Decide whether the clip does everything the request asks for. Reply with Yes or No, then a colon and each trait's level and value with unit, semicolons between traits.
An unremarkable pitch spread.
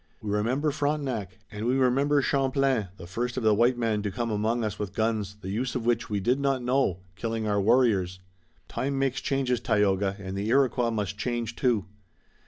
Yes: average, 3.9 semitones